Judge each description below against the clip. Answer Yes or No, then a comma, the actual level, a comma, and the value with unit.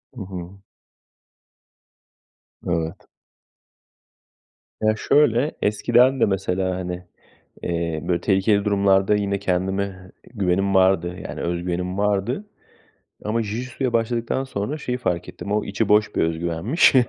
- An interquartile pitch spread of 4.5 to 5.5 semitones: No, average, 3.7 semitones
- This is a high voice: No, low, 100 Hz